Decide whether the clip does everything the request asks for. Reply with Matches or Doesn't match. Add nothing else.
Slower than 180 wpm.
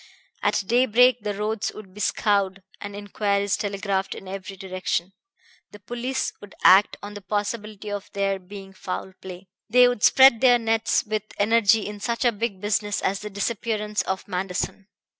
Matches